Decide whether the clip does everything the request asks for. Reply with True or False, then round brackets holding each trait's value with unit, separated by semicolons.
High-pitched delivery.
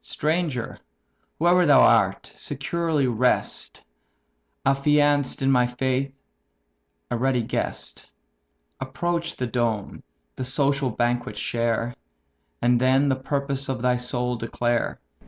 False (130 Hz)